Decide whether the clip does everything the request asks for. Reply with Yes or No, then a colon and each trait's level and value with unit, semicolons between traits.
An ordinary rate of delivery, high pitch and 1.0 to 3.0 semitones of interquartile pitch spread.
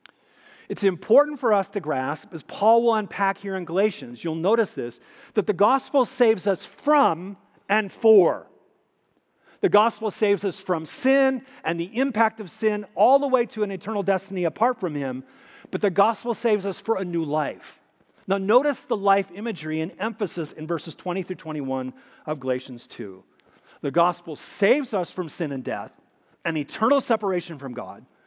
No: average, 175 wpm; high, 195 Hz; average, 5.1 semitones